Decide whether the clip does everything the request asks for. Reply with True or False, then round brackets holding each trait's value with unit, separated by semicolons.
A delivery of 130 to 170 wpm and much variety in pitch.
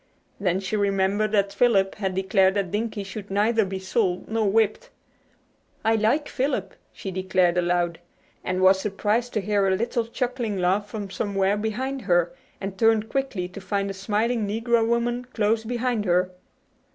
False (165 wpm; 2.9 semitones)